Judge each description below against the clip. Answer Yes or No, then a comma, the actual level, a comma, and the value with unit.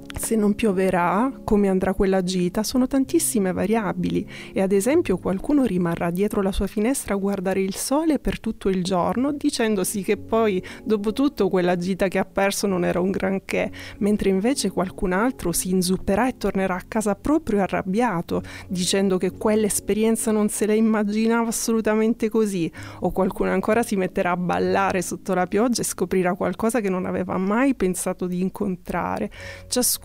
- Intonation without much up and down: No, average, 3.2 semitones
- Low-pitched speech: No, high, 195 Hz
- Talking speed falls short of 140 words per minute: No, average, 165 wpm